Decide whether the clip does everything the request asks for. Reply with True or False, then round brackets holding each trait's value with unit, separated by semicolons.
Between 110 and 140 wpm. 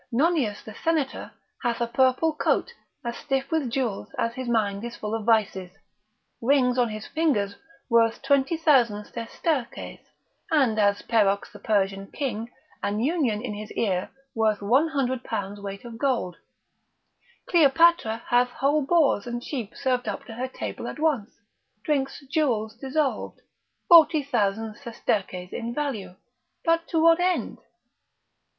True (135 wpm)